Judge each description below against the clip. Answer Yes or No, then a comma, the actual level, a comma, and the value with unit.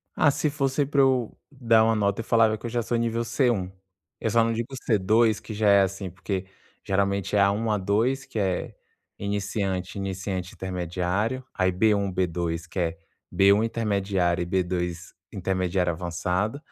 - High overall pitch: No, low, 100 Hz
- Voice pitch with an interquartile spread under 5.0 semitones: Yes, average, 3.6 semitones